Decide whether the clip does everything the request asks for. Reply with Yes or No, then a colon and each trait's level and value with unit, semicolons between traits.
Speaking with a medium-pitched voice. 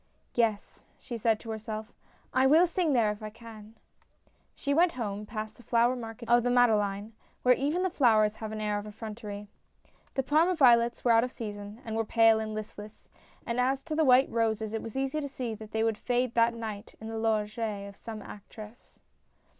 No: high, 225 Hz